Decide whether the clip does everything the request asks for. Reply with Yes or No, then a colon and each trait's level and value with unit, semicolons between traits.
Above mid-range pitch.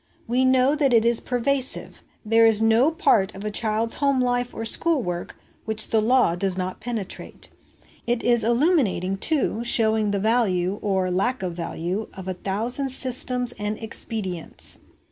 Yes: high, 225 Hz